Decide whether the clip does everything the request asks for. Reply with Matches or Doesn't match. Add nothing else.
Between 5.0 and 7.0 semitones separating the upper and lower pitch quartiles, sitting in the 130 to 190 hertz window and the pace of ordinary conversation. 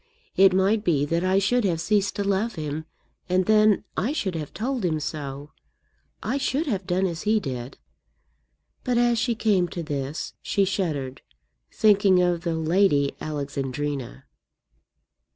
Matches